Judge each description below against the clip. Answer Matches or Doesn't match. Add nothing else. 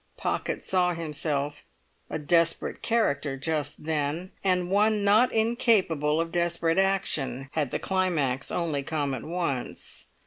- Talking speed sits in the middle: Doesn't match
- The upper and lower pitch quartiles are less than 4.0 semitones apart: Doesn't match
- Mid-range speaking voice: Matches